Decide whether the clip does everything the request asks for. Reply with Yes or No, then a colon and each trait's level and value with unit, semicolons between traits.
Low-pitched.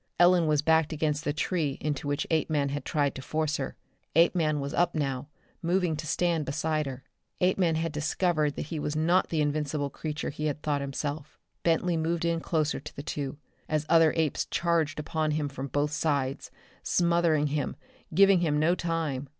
No: medium, 155 Hz